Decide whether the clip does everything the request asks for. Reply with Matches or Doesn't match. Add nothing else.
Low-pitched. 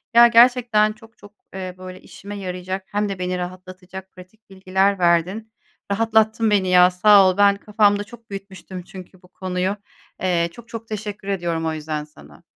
Doesn't match